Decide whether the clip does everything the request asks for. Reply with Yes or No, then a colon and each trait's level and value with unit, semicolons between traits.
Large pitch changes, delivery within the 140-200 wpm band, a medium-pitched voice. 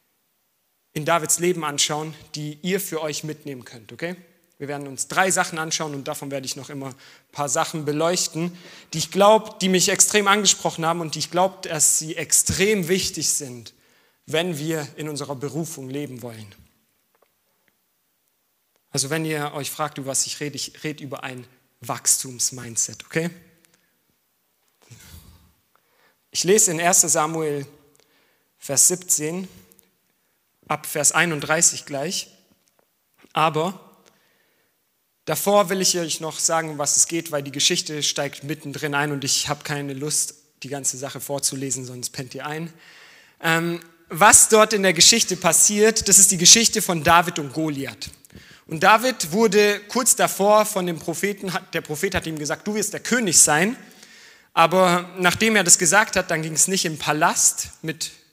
No: average, 4.0 semitones; average, 155 wpm; medium, 160 Hz